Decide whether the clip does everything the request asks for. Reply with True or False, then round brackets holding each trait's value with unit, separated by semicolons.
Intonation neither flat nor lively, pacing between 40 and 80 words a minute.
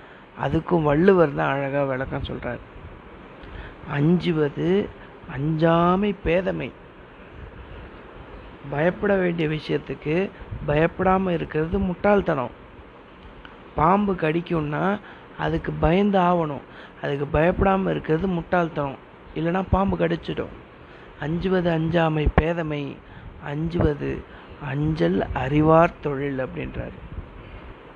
True (3.6 semitones; 75 wpm)